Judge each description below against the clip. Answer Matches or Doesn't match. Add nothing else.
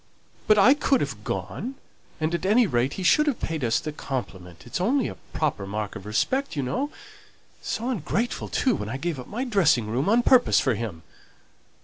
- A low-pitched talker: Doesn't match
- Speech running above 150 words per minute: Matches